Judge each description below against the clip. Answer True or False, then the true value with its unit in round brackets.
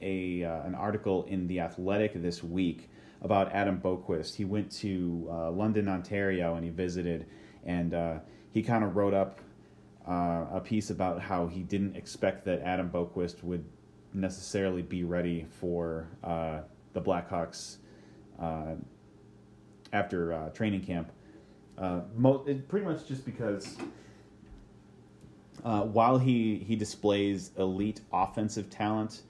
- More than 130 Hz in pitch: False (95 Hz)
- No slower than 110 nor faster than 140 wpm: True (135 wpm)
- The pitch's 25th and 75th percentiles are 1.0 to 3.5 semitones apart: True (3.2 semitones)